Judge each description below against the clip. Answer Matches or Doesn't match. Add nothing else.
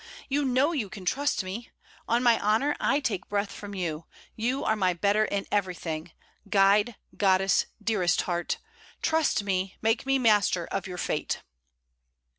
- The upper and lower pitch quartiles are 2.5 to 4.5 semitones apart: Matches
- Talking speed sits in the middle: Matches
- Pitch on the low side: Doesn't match